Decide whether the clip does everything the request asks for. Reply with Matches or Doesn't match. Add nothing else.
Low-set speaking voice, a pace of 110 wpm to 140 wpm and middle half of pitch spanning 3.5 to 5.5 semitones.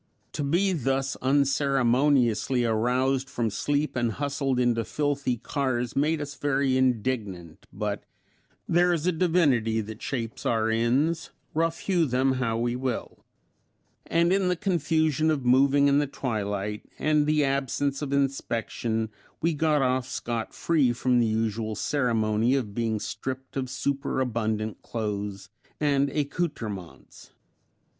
Matches